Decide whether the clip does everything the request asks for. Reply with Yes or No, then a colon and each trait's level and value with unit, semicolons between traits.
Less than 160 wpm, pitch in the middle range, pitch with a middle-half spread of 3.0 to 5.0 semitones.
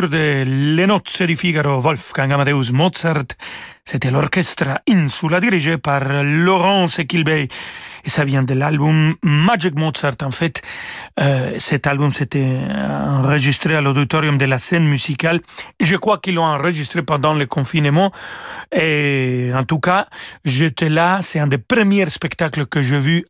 Yes: average, 150 wpm; medium, 155 Hz; average, 3.5 semitones